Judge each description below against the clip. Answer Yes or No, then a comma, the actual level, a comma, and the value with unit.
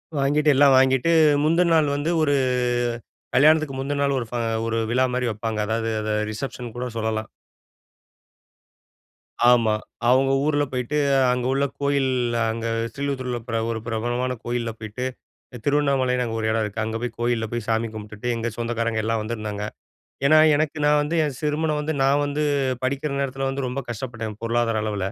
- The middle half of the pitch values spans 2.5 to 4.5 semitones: Yes, average, 3.8 semitones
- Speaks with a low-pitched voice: Yes, low, 125 Hz